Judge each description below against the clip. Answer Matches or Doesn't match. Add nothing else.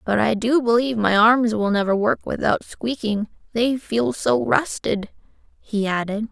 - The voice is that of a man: Doesn't match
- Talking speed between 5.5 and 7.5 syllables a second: Doesn't match